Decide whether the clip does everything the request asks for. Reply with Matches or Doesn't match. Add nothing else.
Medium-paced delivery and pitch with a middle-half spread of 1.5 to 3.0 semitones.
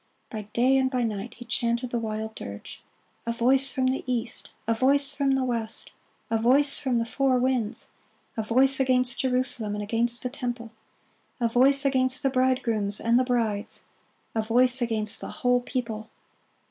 Matches